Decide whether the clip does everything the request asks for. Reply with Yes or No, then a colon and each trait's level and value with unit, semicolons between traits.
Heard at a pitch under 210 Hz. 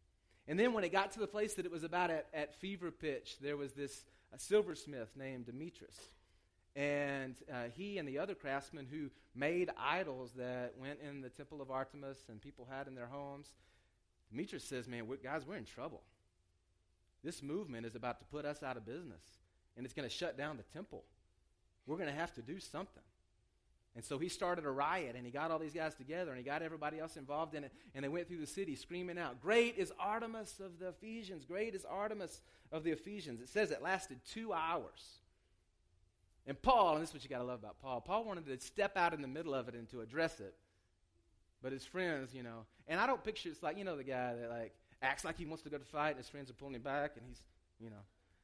Yes: medium, 140 Hz